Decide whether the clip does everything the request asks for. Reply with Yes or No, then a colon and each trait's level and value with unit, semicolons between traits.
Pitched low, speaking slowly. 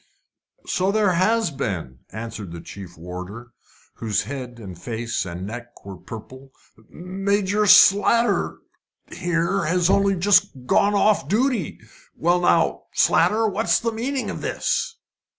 No: medium, 170 Hz; slow, 130 wpm